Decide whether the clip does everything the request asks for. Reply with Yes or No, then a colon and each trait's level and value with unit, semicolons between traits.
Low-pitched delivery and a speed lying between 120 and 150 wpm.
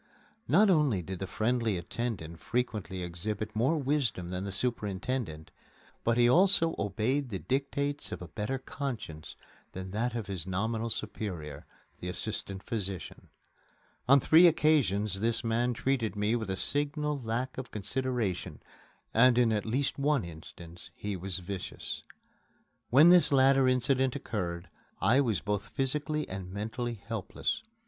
Yes: low, 115 Hz; average, 140 wpm